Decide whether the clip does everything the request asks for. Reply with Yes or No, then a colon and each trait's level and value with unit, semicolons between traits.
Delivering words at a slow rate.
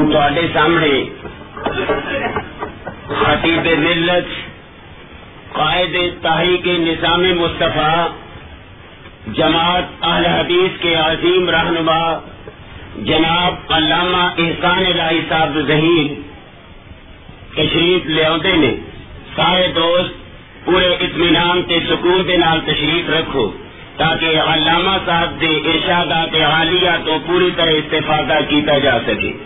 Yes: slow, 100 wpm